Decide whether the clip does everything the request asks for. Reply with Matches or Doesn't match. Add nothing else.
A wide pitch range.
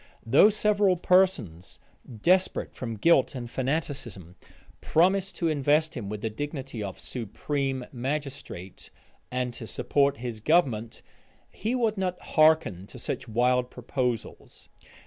Matches